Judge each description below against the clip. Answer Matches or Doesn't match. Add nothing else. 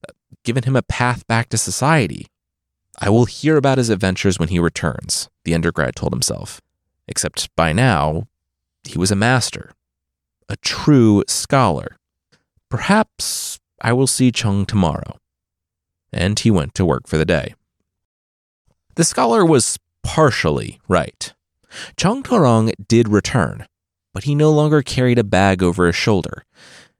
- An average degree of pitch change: Doesn't match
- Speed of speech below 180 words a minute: Matches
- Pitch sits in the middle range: Doesn't match